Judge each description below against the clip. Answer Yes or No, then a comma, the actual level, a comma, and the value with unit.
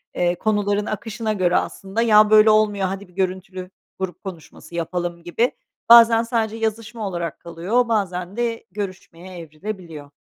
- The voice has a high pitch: Yes, high, 195 Hz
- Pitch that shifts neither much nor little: Yes, average, 3.5 semitones